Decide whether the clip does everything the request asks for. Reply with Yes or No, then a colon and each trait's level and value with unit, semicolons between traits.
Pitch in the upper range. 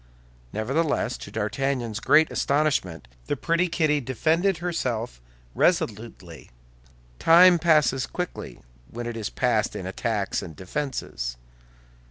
No: low, 135 Hz